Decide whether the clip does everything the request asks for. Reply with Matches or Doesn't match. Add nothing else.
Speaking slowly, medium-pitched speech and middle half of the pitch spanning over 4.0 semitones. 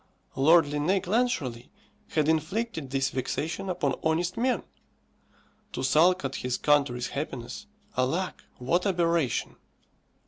Matches